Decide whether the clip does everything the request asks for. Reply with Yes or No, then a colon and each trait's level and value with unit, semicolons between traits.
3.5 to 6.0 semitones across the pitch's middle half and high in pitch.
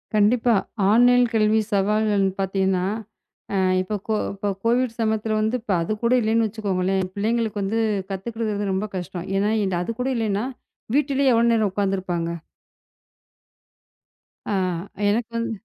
No: average, 2.9 semitones; high, 215 Hz